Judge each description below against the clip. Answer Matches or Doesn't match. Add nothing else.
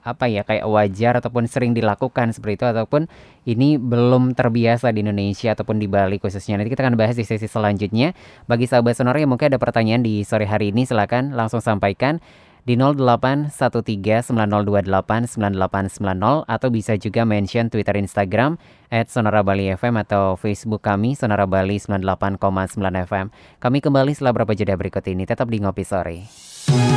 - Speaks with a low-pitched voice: Matches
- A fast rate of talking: Matches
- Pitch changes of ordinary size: Matches